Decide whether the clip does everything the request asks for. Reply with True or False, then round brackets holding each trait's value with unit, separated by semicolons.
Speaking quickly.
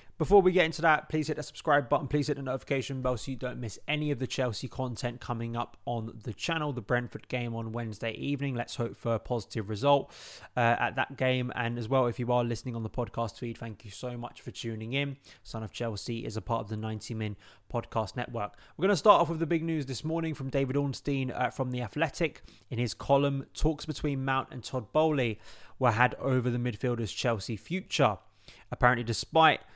True (225 wpm)